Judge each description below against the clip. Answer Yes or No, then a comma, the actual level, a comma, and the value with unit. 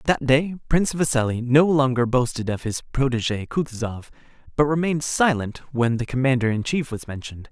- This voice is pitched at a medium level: No, low, 130 Hz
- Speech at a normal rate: Yes, average, 170 wpm